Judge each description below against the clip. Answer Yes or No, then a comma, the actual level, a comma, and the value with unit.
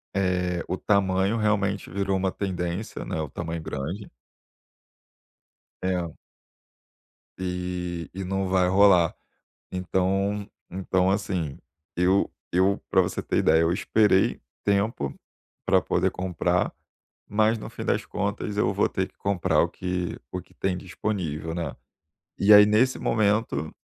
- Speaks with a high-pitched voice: No, very low, 95 Hz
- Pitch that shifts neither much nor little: No, narrow, 2.1 semitones